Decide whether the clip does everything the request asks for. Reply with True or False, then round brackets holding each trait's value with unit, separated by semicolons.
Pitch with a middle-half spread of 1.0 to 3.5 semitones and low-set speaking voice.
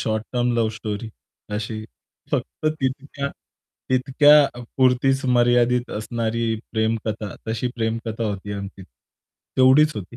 True (2.9 semitones; 115 Hz)